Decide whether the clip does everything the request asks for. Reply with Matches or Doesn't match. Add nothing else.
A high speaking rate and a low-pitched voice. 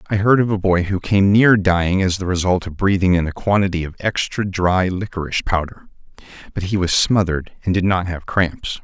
Matches